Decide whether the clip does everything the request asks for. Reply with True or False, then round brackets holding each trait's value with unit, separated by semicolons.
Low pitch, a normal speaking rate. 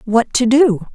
False (235 Hz; 190 wpm)